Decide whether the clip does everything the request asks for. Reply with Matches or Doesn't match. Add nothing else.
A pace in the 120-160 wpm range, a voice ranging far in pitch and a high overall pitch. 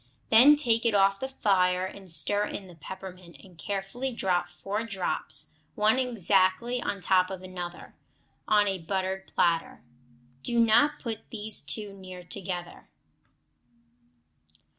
Doesn't match